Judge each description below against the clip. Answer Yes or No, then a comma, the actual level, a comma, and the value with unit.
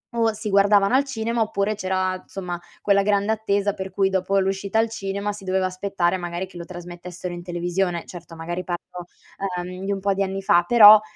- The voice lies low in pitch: No, high, 195 Hz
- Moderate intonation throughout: No, narrow, 2.2 semitones